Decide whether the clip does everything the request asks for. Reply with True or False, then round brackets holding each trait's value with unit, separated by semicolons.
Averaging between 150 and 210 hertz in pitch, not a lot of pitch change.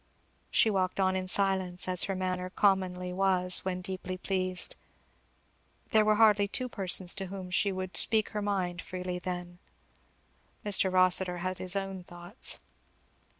True (185 Hz; 1.2 semitones)